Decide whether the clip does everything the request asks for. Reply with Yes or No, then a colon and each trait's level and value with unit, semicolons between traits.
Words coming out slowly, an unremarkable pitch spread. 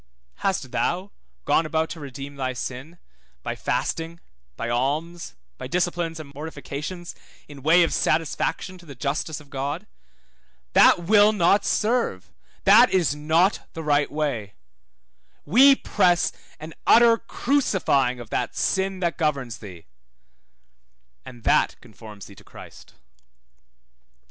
Yes: slow, 130 wpm; average, 4.5 semitones